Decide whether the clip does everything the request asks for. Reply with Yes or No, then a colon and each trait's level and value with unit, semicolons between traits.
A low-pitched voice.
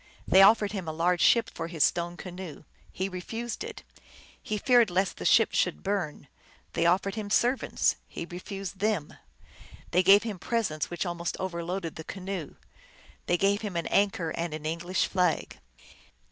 No: medium, 185 Hz